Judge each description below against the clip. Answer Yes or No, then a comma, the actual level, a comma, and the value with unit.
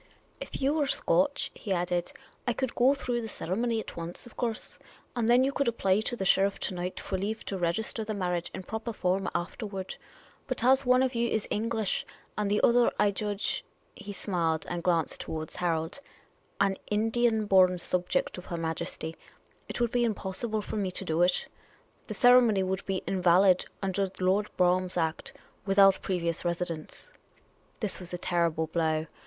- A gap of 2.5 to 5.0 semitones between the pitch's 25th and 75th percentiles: Yes, average, 4.2 semitones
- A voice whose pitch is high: Yes, high, 195 Hz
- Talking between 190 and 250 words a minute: Yes, average, 195 wpm